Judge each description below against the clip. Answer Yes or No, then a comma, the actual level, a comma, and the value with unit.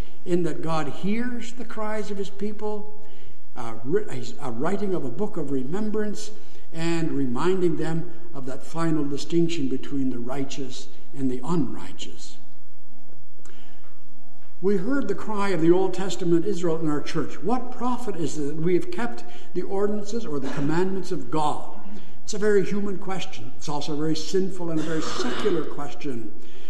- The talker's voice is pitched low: No, medium, 175 Hz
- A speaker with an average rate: Yes, average, 160 wpm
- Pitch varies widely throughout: No, average, 4.9 semitones